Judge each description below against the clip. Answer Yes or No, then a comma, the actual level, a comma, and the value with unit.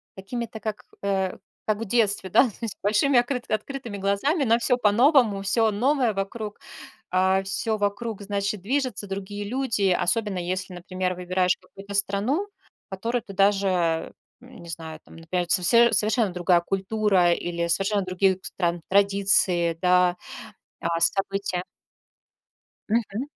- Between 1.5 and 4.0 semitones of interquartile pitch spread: Yes, average, 3.4 semitones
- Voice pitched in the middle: No, high, 200 Hz